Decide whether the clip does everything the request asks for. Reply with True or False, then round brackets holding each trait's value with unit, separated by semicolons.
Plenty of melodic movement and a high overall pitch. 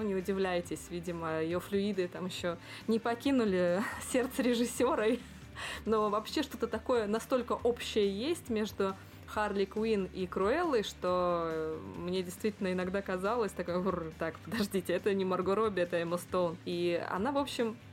False (3.8 semitones; 195 Hz)